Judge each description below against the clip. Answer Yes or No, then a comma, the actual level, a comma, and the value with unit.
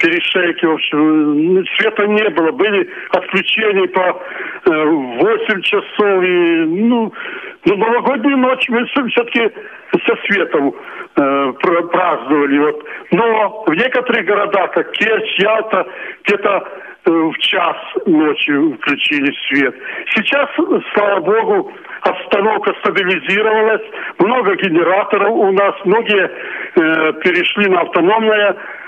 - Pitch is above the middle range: Yes, high, 215 Hz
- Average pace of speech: No, slow, 105 wpm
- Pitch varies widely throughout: Yes, wide, 8.8 semitones